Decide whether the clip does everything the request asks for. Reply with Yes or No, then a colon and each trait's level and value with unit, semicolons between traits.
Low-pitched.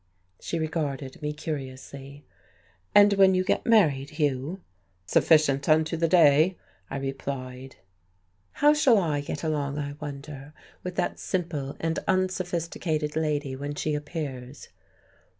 No: medium, 150 Hz